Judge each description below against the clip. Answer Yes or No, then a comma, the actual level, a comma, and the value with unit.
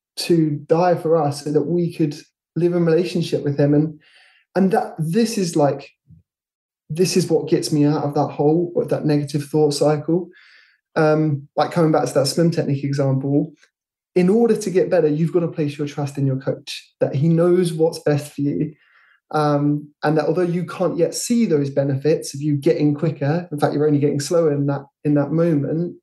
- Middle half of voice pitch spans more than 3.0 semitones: No, narrow, 2.5 semitones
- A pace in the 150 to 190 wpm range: No, fast, 205 wpm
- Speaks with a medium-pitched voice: Yes, medium, 155 Hz